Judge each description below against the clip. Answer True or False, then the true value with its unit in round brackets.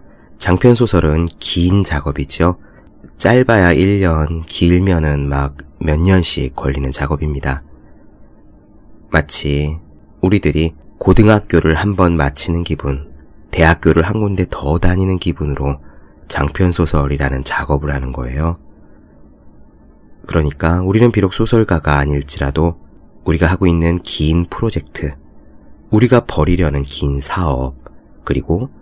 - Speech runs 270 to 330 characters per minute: False (250 characters per minute)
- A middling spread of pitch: True (4.1 semitones)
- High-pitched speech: False (80 Hz)